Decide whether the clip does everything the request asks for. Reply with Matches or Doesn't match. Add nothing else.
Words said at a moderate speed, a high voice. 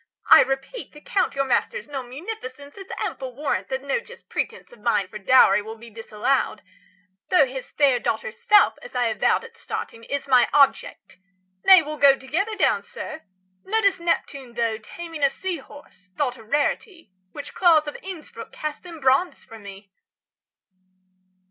Matches